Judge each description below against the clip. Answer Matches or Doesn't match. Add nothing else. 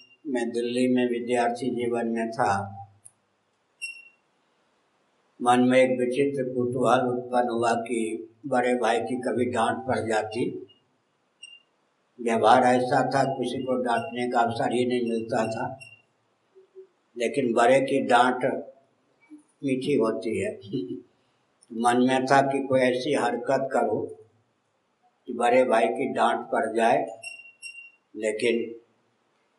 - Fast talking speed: Doesn't match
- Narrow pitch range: Matches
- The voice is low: Matches